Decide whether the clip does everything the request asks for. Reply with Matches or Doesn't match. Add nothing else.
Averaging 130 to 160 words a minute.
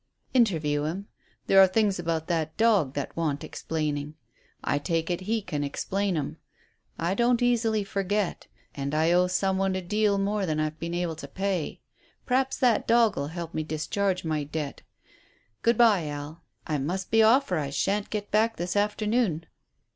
Doesn't match